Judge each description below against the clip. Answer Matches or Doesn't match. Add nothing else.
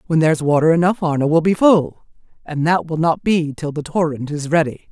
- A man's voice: Doesn't match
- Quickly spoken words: Matches